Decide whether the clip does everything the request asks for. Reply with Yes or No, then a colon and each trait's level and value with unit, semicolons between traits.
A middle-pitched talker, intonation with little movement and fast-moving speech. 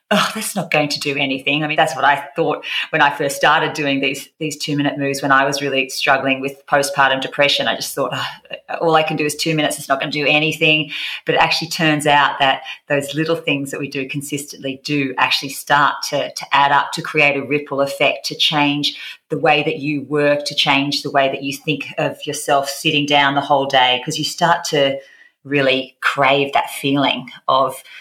Yes: medium, 145 Hz; narrow, 1.6 semitones; fast, 220 wpm